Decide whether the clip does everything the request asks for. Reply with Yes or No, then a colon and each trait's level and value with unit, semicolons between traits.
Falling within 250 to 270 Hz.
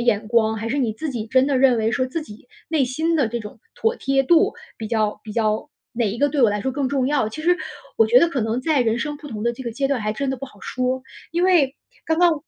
Yes: very high, 255 Hz